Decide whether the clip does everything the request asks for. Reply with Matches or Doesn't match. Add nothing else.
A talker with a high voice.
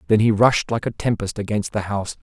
Doesn't match